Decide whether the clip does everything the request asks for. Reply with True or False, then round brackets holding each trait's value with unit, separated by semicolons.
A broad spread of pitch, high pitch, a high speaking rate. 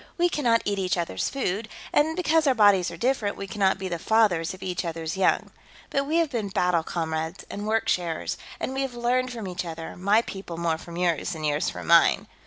True (5.8 semitones; 195 Hz; 215 wpm)